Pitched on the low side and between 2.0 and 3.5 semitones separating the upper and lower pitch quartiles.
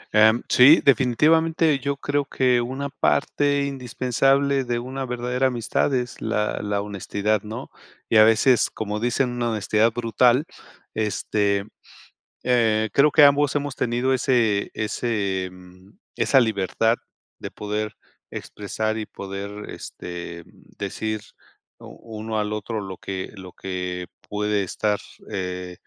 No: low, 110 Hz; average, 4.0 semitones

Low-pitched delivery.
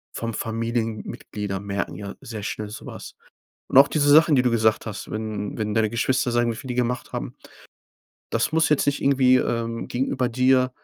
Yes: low, 115 Hz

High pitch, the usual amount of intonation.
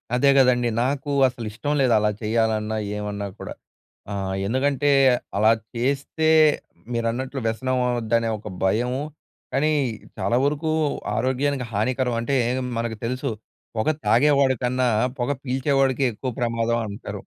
No: low, 125 Hz; average, 3.0 semitones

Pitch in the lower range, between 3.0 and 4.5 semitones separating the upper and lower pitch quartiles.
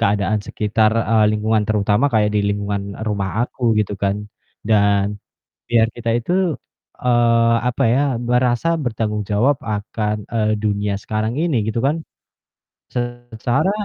No: low, 110 Hz; narrow, 2.5 semitones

